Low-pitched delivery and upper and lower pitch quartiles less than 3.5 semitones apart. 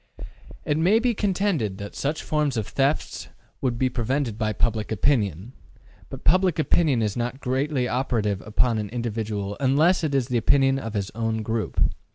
No: low, 125 Hz; average, 4.8 semitones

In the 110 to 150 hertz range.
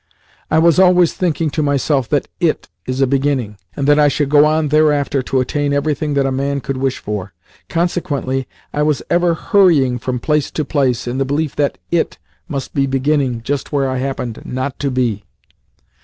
Yes: medium, 140 Hz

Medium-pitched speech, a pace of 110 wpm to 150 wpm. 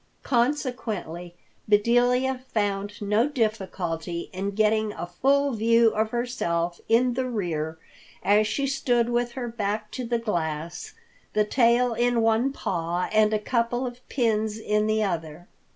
No: high, 220 Hz; average, 140 wpm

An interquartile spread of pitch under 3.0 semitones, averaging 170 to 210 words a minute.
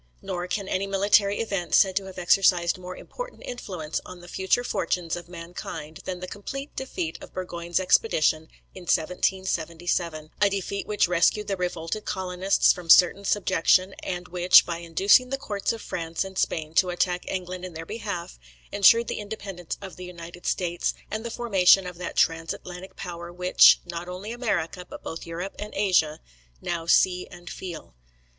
Yes: narrow, 2.4 semitones; average, 175 wpm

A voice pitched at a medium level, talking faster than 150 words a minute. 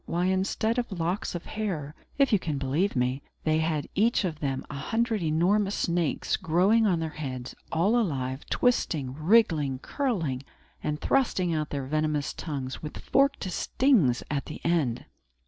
Yes: medium, 165 Hz; average, 160 wpm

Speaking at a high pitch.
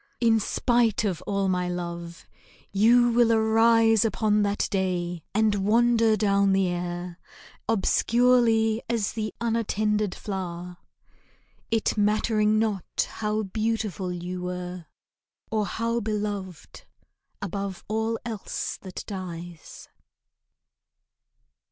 Yes: high, 210 Hz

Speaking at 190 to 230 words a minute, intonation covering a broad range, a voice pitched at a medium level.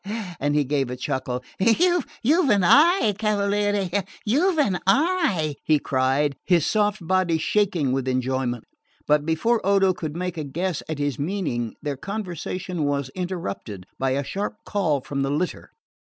No: average, 155 wpm; wide, 6.5 semitones; medium, 170 Hz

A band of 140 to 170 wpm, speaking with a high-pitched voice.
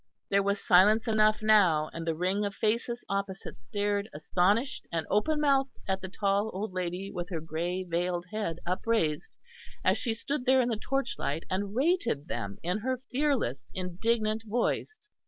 Yes: average, 165 wpm; high, 200 Hz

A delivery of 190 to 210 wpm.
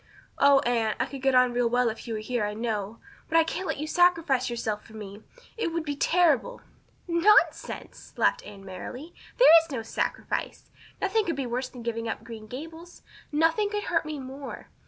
Yes: average, 200 wpm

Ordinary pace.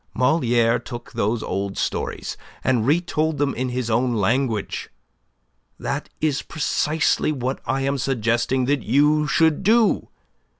No: slow, 130 wpm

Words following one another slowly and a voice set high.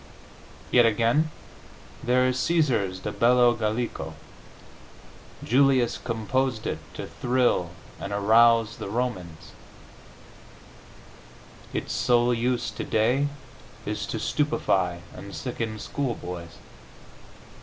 No: slow, 90 wpm; low, 115 Hz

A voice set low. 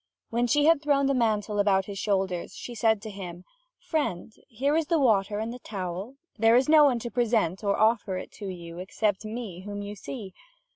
No: high, 215 Hz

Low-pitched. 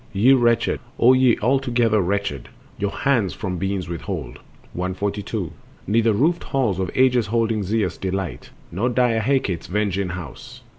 Yes: low, 105 Hz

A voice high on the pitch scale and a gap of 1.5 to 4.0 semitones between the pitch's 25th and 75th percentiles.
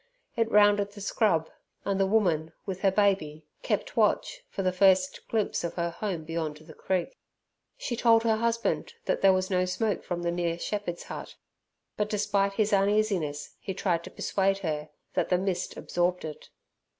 Yes: high, 195 Hz; average, 3.4 semitones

